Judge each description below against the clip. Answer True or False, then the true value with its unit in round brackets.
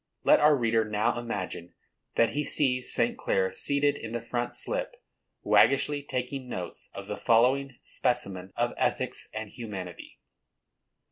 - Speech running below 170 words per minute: True (140 wpm)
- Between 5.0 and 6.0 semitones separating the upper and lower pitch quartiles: False (4.2 semitones)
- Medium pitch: False (120 Hz)